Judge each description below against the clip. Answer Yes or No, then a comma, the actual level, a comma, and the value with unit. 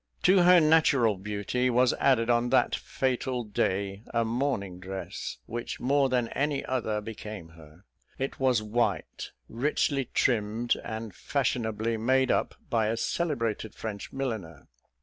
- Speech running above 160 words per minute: No, slow, 135 wpm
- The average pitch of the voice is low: Yes, low, 115 Hz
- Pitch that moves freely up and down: No, average, 3.8 semitones